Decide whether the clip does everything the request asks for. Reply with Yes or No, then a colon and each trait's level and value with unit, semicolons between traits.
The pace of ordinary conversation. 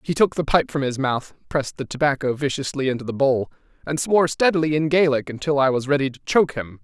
No: fast, 230 wpm